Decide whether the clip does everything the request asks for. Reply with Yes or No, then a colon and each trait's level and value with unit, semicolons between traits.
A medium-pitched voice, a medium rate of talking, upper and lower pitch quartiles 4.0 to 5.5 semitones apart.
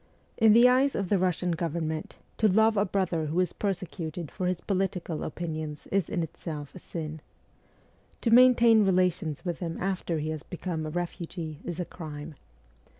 No: medium, 175 Hz; average, 180 wpm; average, 3.6 semitones